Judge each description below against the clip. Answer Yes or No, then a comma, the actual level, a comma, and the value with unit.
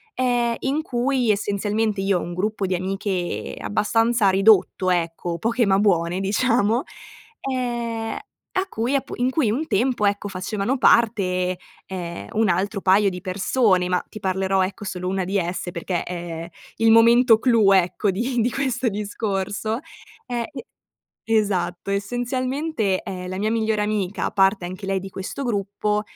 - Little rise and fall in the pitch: No, average, 3.8 semitones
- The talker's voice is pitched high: Yes, high, 205 Hz